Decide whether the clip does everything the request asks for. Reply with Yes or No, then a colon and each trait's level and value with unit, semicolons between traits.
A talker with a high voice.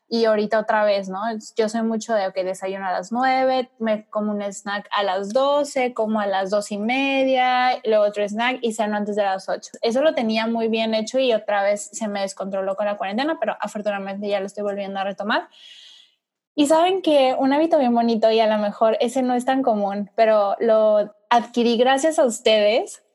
Yes: high, 220 Hz